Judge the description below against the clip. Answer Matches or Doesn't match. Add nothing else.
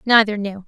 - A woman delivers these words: Matches